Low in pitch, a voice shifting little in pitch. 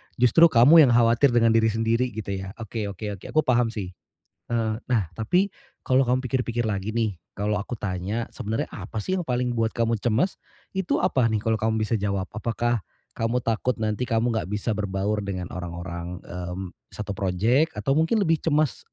No: low, 115 Hz; average, 3.3 semitones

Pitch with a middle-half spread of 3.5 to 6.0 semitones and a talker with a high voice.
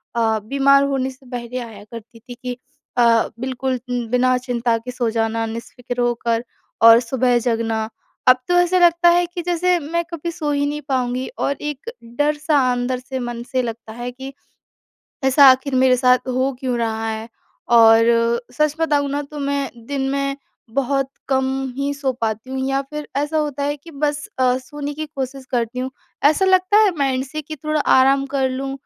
No: average, 3.1 semitones; very high, 265 Hz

